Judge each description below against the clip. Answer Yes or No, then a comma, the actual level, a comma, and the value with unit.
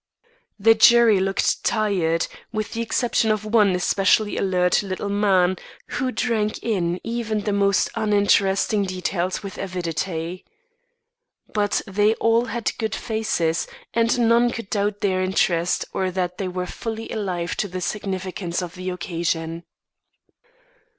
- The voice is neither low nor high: No, high, 200 Hz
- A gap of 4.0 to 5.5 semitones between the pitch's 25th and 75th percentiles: No, average, 3.1 semitones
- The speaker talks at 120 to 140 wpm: Yes, slow, 135 wpm